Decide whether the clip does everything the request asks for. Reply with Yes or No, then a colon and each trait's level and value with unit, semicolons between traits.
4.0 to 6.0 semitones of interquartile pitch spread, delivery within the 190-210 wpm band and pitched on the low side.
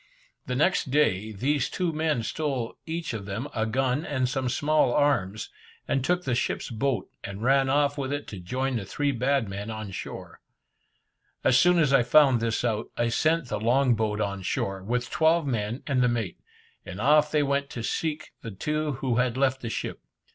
Yes: average, 4.4 semitones; average, 200 wpm; low, 130 Hz